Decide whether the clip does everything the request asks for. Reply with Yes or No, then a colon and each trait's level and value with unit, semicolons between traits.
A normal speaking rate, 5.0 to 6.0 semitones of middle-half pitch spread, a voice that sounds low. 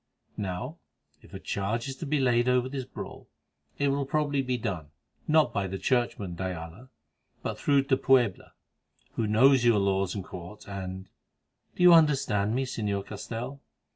Yes: average, 165 wpm; wide, 5.6 semitones; low, 120 Hz